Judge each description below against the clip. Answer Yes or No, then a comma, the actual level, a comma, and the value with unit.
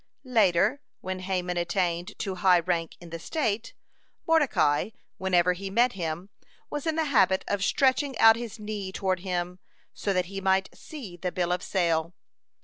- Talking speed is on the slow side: No, average, 165 wpm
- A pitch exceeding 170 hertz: Yes, high, 190 Hz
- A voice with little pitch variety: No, average, 3.8 semitones